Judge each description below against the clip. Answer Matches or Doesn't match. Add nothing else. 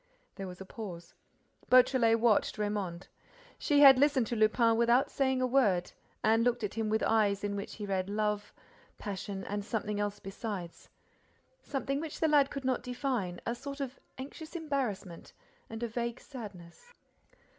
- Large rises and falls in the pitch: Doesn't match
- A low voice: Doesn't match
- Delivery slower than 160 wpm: Doesn't match